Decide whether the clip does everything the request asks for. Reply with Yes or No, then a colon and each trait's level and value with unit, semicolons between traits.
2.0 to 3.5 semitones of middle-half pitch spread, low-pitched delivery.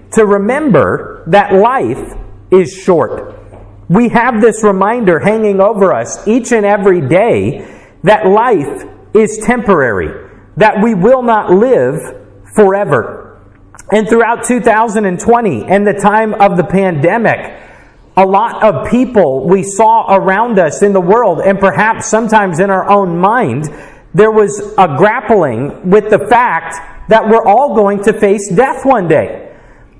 No: average, 2.7 semitones; high, 205 Hz